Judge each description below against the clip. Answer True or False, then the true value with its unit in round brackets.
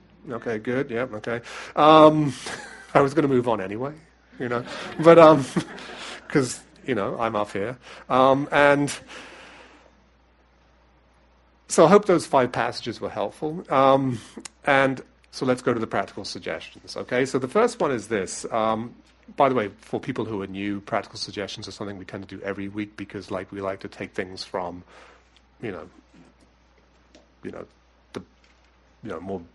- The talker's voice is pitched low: True (105 Hz)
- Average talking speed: True (170 wpm)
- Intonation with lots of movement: True (6.6 semitones)